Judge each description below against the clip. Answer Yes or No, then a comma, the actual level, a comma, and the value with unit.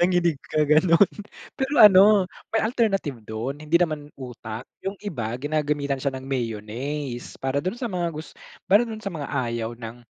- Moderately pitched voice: Yes, medium, 150 Hz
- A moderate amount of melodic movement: No, wide, 6.6 semitones